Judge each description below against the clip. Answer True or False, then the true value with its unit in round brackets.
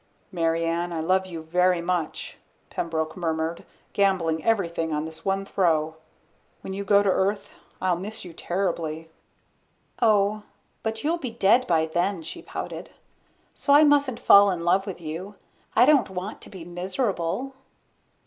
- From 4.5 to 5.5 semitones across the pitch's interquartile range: False (3.5 semitones)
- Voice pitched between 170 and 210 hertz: True (185 Hz)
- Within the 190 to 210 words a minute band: False (155 wpm)